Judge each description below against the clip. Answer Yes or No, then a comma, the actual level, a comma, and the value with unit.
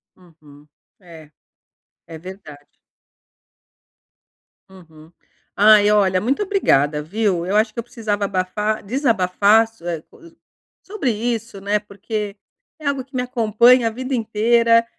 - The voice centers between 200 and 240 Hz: Yes, high, 210 Hz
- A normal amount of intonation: Yes, average, 4.1 semitones